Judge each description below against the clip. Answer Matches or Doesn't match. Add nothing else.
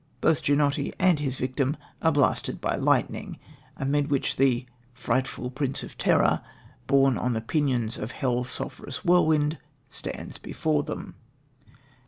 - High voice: Doesn't match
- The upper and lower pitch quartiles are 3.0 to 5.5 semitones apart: Doesn't match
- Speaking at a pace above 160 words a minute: Doesn't match